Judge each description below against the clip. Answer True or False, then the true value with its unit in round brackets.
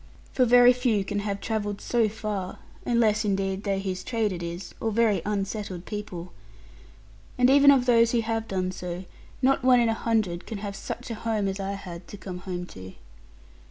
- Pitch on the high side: True (205 Hz)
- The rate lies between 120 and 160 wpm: False (195 wpm)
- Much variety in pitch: False (3.3 semitones)